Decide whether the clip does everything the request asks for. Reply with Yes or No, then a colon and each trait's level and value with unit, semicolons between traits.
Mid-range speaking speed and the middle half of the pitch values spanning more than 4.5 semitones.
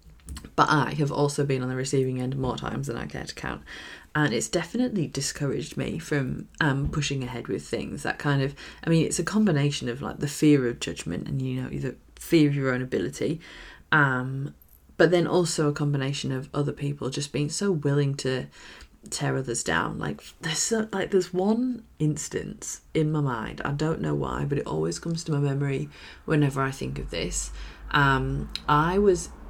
No: average, 195 wpm; average, 3.2 semitones